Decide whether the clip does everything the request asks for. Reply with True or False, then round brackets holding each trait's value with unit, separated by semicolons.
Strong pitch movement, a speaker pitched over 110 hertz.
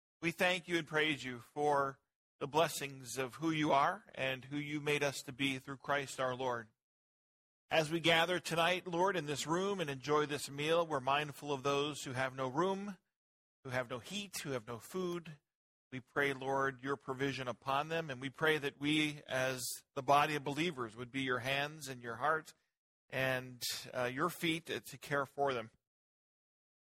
False (3.2 semitones; 140 Hz)